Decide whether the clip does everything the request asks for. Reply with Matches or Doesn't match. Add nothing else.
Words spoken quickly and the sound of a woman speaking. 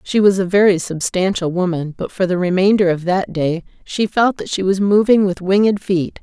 Matches